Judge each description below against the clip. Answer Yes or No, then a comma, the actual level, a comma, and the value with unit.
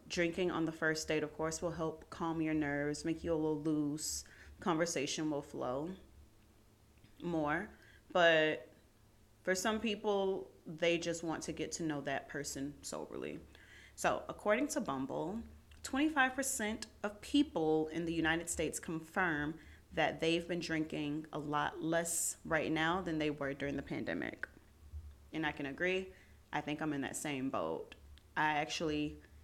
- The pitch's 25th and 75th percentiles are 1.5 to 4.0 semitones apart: Yes, average, 3.2 semitones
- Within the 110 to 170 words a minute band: Yes, average, 155 wpm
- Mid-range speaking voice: Yes, medium, 155 Hz